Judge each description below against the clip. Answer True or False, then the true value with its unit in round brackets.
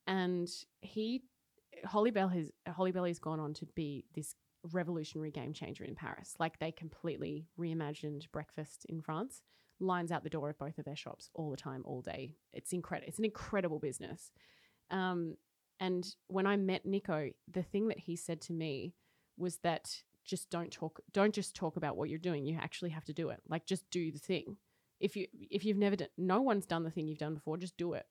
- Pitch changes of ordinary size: True (3.2 semitones)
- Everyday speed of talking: False (210 wpm)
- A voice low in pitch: False (170 Hz)